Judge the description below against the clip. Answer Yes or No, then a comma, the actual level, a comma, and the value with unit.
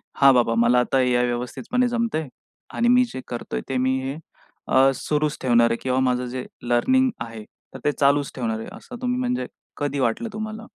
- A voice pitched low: Yes, low, 130 Hz